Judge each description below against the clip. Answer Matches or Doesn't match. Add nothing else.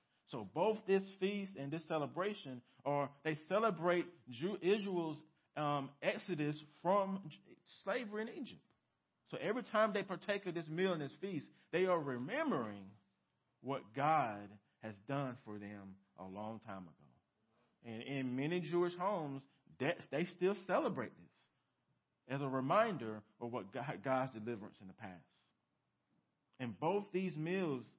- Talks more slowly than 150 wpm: Matches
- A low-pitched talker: Doesn't match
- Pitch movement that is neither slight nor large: Doesn't match